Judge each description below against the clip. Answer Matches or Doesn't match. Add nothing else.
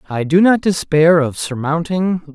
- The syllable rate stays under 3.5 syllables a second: Doesn't match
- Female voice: Doesn't match